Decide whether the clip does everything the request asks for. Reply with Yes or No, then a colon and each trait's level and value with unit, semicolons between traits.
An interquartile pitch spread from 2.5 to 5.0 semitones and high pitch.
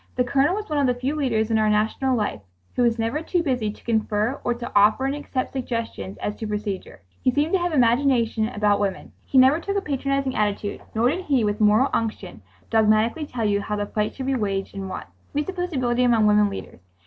Yes: average, 4.3 semitones; high, 235 Hz